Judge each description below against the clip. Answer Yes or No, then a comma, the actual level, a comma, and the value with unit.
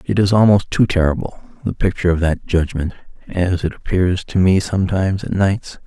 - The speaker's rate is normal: Yes, average, 185 wpm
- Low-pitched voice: Yes, very low, 90 Hz